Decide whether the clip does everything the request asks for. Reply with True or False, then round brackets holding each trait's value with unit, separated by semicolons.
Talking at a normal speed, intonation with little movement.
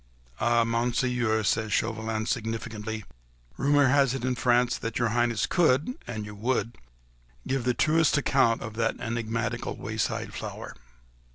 False (125 wpm; 2.3 semitones)